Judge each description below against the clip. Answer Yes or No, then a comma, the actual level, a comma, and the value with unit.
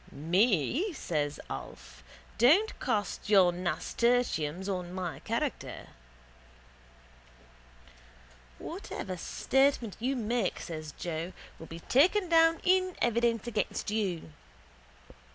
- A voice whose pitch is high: Yes, high, 205 Hz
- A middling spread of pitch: No, wide, 6.6 semitones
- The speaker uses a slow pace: Yes, slow, 95 wpm